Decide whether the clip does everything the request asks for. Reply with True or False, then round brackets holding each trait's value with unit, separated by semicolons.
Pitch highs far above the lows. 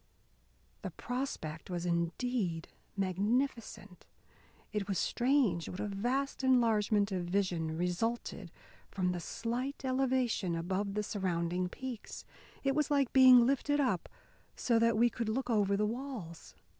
True (5.8 semitones)